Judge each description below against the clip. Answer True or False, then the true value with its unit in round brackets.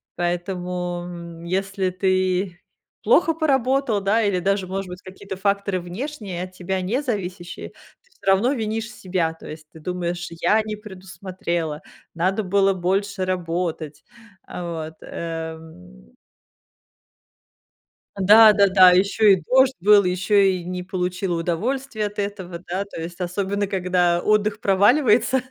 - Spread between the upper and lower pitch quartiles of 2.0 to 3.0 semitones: True (2.6 semitones)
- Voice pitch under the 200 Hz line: True (185 Hz)